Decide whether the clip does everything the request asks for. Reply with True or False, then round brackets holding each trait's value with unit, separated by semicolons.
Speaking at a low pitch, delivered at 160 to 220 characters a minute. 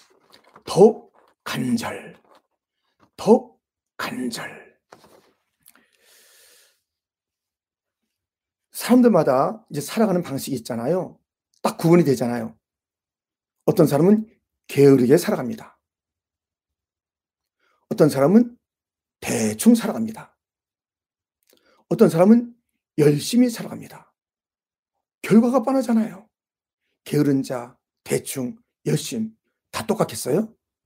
False (185 Hz; 180 characters per minute)